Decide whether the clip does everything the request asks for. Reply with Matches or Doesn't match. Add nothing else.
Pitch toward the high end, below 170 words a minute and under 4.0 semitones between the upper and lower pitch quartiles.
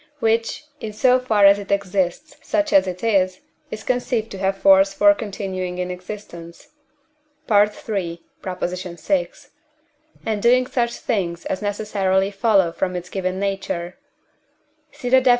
Matches